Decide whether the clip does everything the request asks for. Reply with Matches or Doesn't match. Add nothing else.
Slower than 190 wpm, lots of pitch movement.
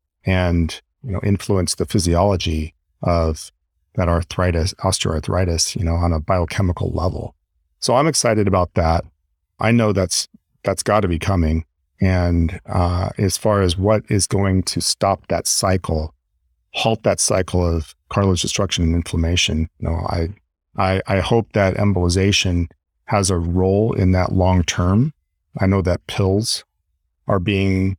Doesn't match